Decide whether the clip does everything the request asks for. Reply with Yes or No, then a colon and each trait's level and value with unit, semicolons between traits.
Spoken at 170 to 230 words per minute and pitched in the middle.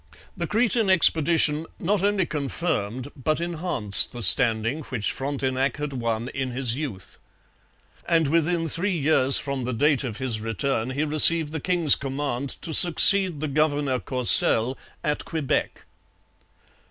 No: average, 140 wpm; medium, 145 Hz